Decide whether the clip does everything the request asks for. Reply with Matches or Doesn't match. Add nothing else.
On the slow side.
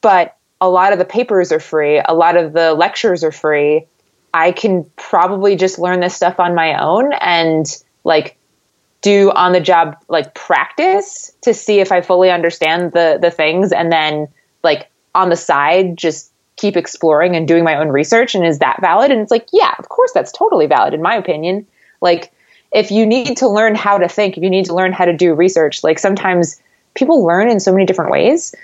Doesn't match